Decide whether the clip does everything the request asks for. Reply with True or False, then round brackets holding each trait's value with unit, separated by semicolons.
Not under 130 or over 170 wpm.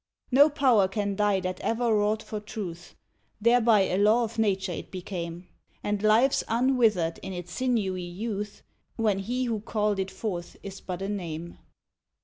True (160 wpm)